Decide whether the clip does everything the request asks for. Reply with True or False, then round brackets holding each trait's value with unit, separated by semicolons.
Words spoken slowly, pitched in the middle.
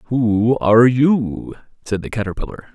False (130 wpm; 115 Hz)